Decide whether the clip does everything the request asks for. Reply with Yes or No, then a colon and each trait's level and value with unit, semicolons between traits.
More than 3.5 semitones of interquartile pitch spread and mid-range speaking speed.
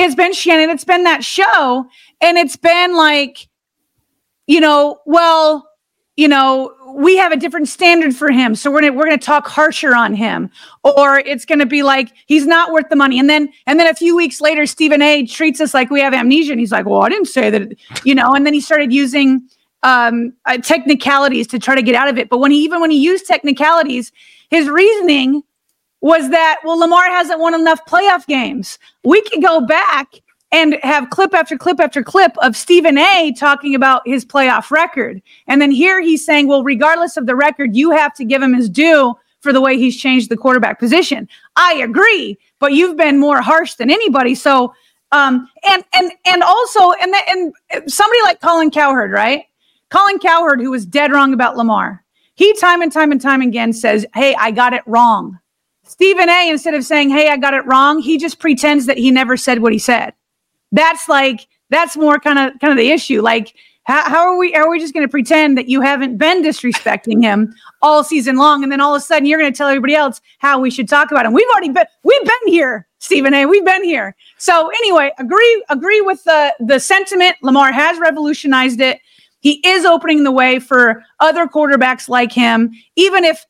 No: average, 3.9 semitones; fast, 210 wpm